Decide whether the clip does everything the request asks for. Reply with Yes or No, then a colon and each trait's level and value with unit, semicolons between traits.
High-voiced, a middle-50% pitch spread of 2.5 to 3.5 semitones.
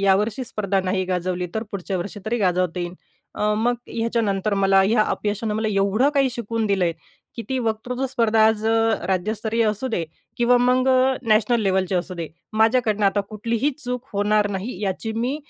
Yes: high, 215 Hz; average, 3.2 semitones